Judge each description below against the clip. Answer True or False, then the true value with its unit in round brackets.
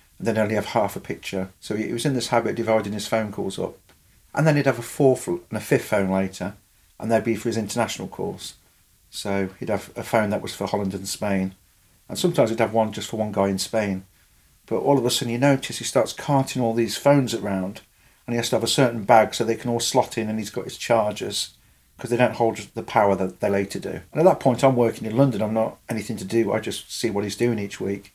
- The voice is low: True (110 Hz)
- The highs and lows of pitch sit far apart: False (3.5 semitones)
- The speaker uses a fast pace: True (260 wpm)